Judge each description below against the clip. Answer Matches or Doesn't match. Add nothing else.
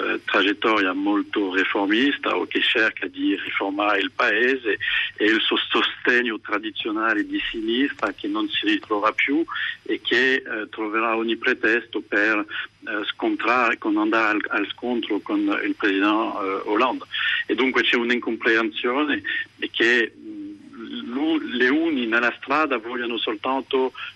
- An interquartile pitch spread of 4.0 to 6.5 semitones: Doesn't match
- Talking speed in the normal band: Matches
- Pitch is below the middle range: Doesn't match